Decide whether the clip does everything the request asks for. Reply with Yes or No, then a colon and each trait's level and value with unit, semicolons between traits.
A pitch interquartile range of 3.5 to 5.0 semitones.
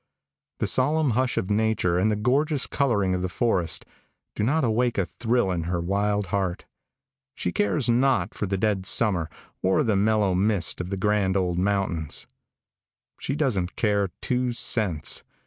Yes: average, 4.4 semitones